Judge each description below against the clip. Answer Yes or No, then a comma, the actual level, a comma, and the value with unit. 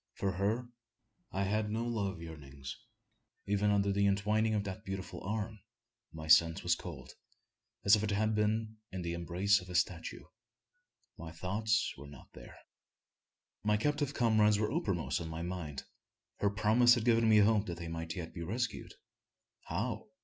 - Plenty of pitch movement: No, average, 4.1 semitones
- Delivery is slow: No, average, 170 wpm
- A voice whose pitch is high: No, low, 100 Hz